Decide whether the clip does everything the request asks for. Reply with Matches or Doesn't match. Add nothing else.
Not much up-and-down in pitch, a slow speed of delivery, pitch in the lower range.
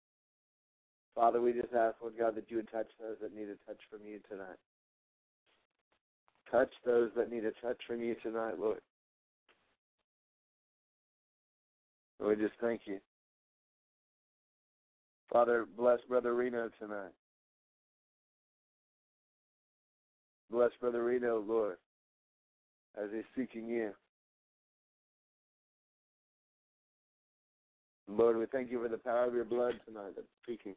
Matches